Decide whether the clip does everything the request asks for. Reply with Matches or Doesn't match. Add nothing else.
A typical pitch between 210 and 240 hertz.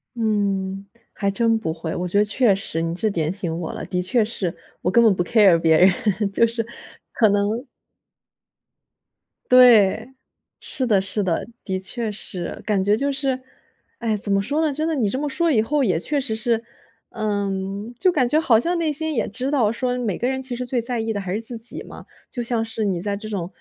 Matches